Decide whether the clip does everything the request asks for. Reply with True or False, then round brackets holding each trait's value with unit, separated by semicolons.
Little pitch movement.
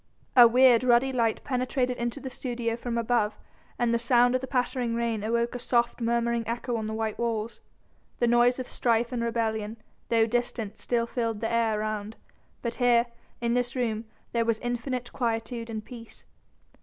True (1.3 semitones)